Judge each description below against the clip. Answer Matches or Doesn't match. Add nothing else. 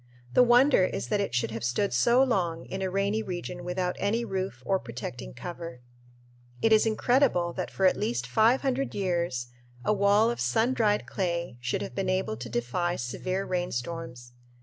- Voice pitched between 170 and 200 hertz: Matches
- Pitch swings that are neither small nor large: Doesn't match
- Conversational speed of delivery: Matches